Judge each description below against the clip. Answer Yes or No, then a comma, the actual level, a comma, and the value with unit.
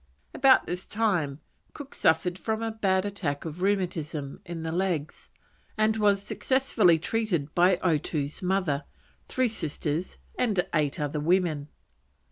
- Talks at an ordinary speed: No, slow, 130 wpm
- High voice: No, medium, 180 Hz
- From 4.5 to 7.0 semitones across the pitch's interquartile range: Yes, average, 5.0 semitones